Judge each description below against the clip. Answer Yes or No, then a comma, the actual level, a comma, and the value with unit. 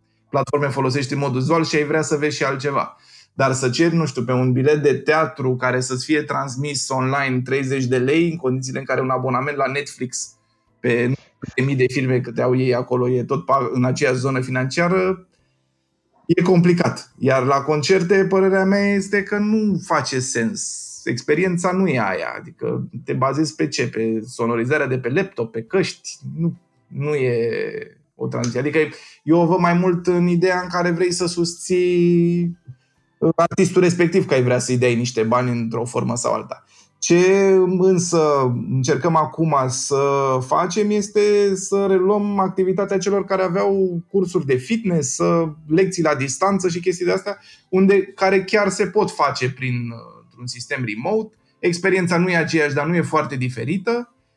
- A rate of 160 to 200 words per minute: Yes, fast, 170 wpm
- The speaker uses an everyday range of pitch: No, wide, 6.1 semitones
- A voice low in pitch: No, medium, 155 Hz